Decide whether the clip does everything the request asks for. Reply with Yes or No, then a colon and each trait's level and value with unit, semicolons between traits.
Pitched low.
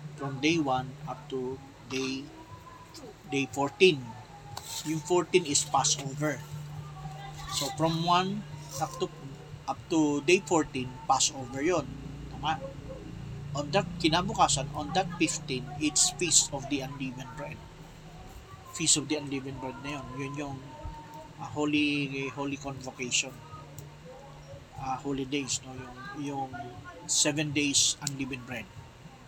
No: medium, 145 Hz